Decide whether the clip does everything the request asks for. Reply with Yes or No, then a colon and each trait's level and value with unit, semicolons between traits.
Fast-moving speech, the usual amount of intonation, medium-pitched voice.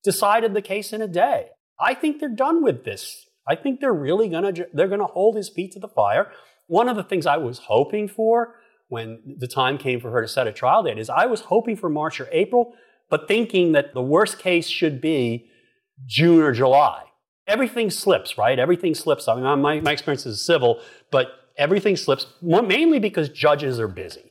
No: fast, 210 wpm; wide, 7.7 semitones; medium, 175 Hz